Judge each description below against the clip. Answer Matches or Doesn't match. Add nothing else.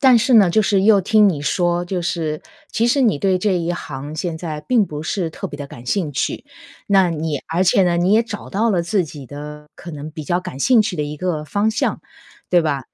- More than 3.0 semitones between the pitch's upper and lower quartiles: Matches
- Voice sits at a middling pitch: Matches